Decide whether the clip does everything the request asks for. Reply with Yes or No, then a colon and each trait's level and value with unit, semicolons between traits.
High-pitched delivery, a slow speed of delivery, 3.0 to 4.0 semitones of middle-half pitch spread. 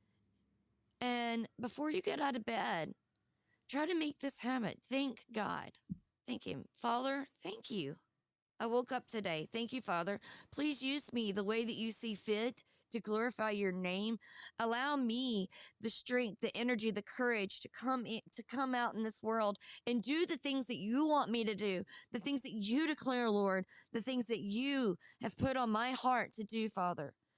No: high, 230 Hz; average, 185 wpm; average, 3.5 semitones